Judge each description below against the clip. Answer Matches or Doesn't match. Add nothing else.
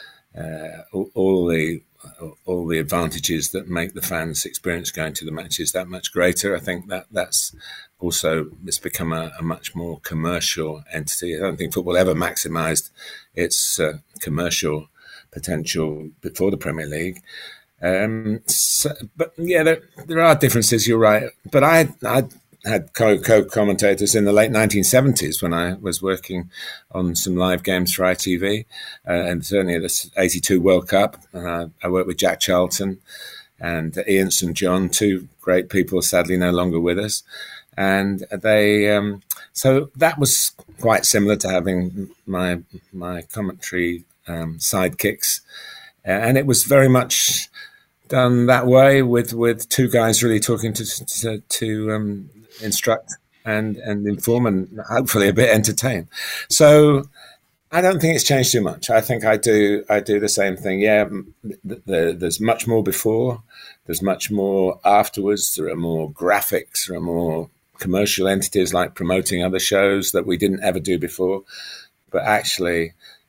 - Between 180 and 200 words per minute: Doesn't match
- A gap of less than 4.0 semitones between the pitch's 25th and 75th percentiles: Doesn't match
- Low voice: Matches